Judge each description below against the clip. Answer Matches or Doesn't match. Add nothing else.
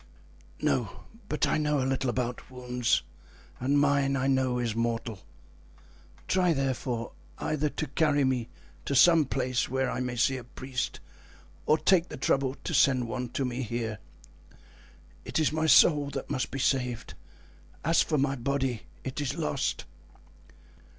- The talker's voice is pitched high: Doesn't match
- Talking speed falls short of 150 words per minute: Doesn't match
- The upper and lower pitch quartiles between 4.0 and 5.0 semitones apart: Doesn't match